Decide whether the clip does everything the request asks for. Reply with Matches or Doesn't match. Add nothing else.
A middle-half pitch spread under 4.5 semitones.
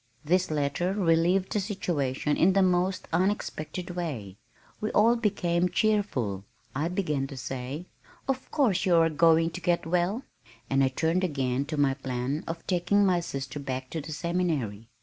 Doesn't match